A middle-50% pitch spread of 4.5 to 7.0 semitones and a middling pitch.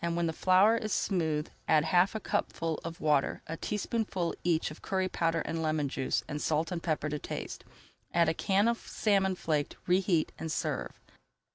No: average, 3.3 semitones; medium, 165 Hz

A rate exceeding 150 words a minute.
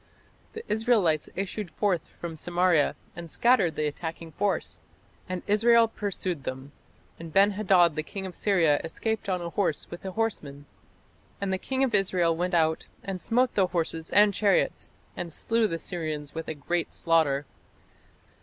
Yes: average, 165 wpm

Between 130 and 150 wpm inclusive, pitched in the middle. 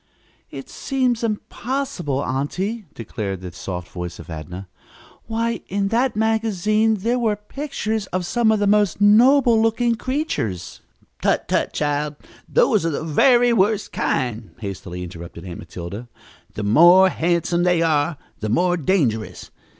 Yes: average, 140 wpm; medium, 180 Hz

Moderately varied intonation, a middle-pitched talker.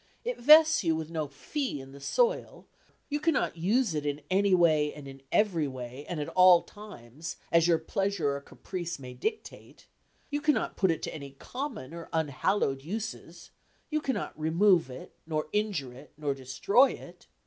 No: wide, 6.6 semitones; medium, 165 Hz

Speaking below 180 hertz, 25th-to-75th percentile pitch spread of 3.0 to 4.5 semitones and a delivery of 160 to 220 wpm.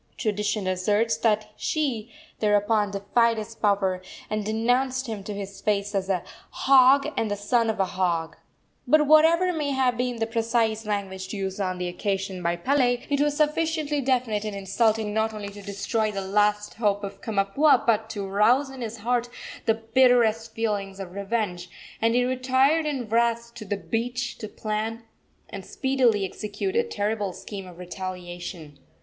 No: high, 220 Hz; average, 3.6 semitones; average, 165 wpm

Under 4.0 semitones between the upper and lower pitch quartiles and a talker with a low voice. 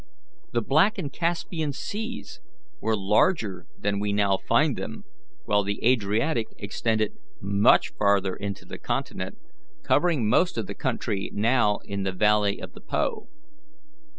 No: average, 4.9 semitones; low, 105 Hz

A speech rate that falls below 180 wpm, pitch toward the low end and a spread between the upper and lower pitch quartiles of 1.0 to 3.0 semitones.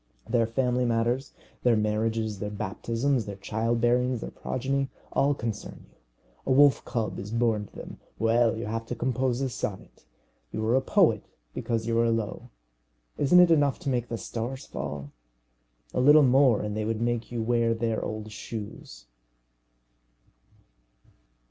Yes: average, 160 wpm; low, 115 Hz; narrow, 2.4 semitones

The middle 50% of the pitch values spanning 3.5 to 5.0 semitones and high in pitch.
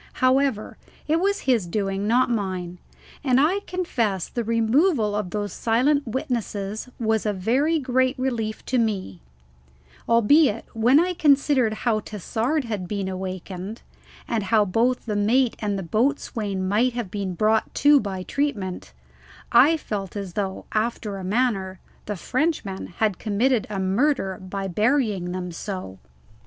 Yes: average, 4.7 semitones; high, 220 Hz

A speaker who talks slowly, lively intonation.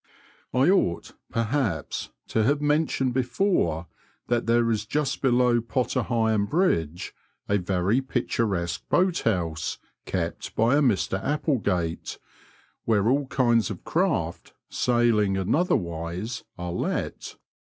Yes: slow, 120 wpm; wide, 6.3 semitones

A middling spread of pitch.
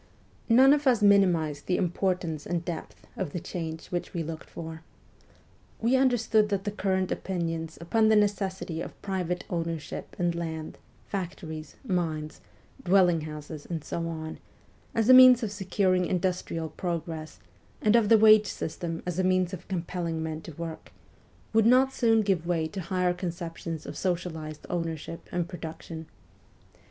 Yes: average, 3.3 semitones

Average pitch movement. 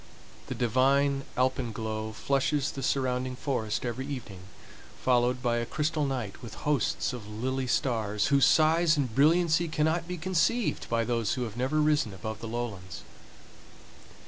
Yes: average, 4.2 semitones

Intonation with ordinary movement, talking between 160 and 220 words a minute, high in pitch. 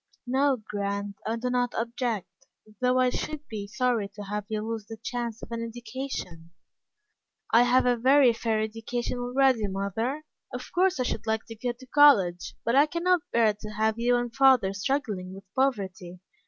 Yes: average, 3.4 semitones; average, 175 wpm; high, 230 Hz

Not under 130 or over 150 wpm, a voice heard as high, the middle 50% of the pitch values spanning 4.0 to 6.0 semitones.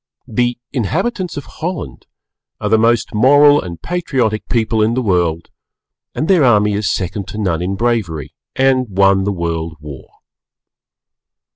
No: average, 145 wpm; low, 110 Hz; wide, 5.5 semitones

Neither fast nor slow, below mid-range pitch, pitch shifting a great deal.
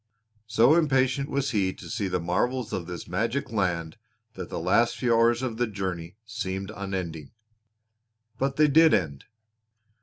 Yes: average, 155 wpm; low, 110 Hz; wide, 5.9 semitones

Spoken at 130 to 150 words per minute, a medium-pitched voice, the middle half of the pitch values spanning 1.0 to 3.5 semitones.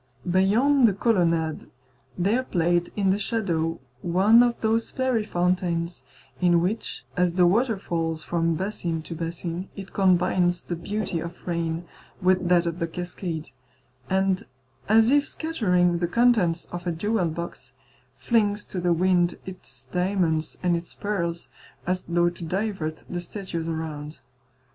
Yes: average, 145 wpm; medium, 180 Hz; average, 3.0 semitones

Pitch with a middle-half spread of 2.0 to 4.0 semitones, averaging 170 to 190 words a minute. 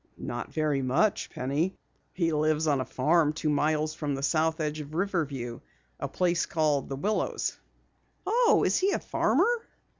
No: average, 3.1 semitones; average, 160 wpm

